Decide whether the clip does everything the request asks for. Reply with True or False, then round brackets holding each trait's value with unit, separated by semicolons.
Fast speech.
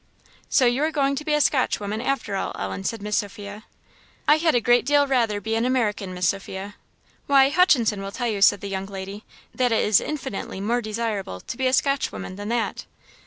True (210 wpm)